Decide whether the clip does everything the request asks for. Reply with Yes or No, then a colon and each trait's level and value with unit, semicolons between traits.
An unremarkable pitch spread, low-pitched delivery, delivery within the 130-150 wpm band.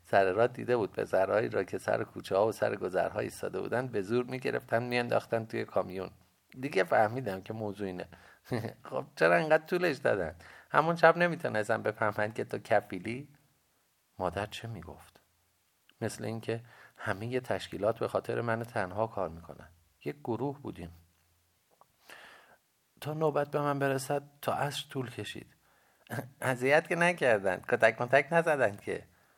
No: wide, 5.9 semitones; low, 115 Hz; average, 145 wpm